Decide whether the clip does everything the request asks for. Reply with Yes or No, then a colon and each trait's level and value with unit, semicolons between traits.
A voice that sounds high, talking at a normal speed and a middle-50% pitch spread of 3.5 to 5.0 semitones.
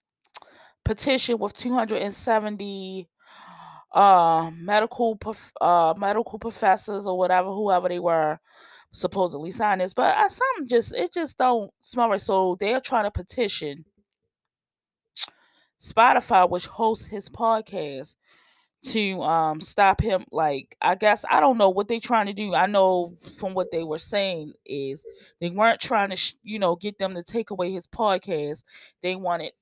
Yes: high, 200 Hz; average, 160 wpm; average, 4.1 semitones